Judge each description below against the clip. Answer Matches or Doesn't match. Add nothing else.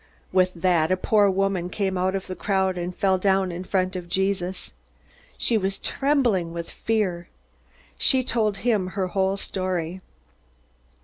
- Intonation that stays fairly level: Matches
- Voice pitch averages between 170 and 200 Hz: Matches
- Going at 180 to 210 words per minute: Doesn't match